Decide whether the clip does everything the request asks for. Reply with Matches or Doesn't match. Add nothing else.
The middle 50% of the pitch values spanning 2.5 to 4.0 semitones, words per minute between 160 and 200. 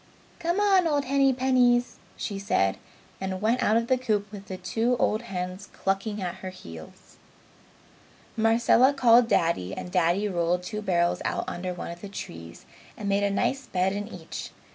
Doesn't match